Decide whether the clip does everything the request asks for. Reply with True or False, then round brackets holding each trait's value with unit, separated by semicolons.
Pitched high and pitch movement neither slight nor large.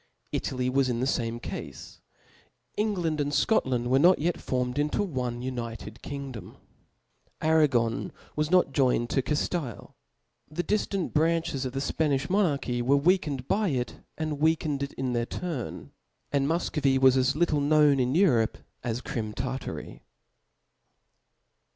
False (140 Hz; 4.0 semitones)